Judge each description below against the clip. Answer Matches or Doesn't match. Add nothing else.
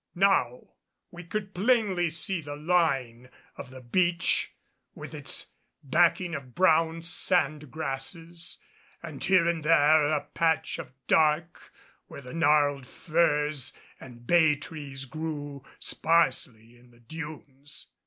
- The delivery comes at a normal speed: Doesn't match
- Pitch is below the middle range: Doesn't match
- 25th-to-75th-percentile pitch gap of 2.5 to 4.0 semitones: Matches